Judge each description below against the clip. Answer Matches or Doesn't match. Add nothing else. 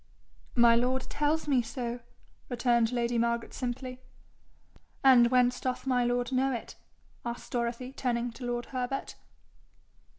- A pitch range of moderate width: Doesn't match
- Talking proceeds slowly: Matches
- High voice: Matches